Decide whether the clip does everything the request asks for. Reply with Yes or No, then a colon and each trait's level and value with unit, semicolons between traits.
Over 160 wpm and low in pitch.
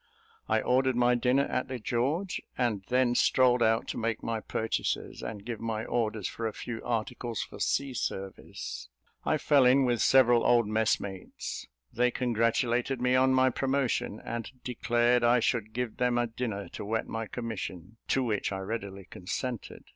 Yes: average, 170 wpm; low, 120 Hz